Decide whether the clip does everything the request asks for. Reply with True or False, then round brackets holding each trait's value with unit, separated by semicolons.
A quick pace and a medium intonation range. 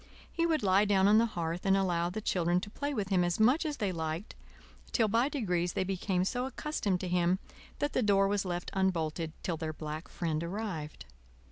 True (210 wpm; 3.9 semitones)